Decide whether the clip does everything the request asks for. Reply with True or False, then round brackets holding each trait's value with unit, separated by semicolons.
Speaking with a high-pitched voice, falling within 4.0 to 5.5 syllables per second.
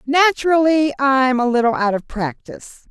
True (265 Hz; 4.9 syllables/s)